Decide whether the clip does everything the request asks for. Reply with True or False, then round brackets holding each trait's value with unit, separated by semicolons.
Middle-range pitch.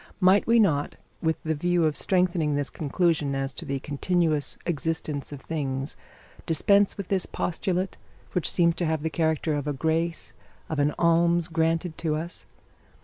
True (160 Hz)